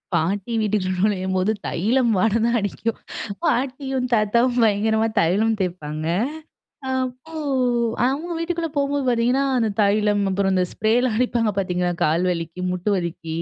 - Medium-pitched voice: No, high, 215 Hz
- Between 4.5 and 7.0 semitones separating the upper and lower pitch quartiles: Yes, average, 5.0 semitones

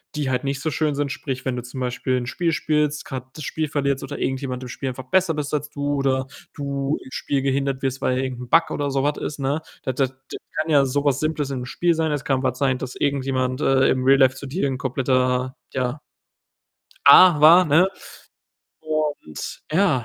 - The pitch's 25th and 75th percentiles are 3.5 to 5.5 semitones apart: No, narrow, 2.4 semitones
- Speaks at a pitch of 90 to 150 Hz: Yes, low, 135 Hz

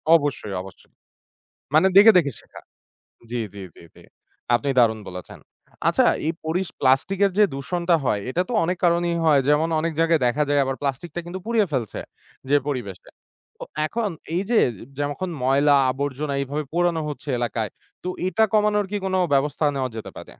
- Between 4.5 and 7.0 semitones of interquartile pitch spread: Yes, average, 4.9 semitones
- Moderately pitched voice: Yes, medium, 150 Hz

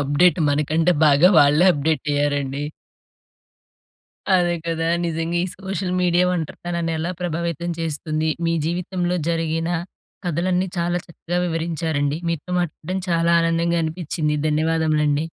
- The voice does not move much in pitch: Yes, narrow, 2.1 semitones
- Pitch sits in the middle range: Yes, medium, 165 Hz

